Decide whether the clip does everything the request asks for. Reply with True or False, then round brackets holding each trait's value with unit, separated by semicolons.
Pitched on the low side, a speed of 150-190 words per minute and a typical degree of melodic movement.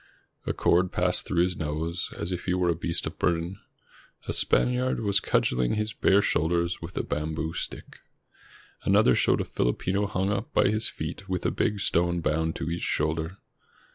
True (85 Hz; 180 wpm; 3.2 semitones)